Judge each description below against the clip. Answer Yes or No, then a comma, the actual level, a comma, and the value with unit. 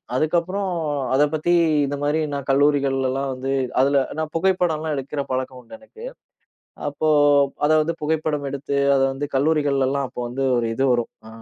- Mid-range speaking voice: Yes, medium, 145 Hz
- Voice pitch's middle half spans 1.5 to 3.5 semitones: Yes, average, 2.8 semitones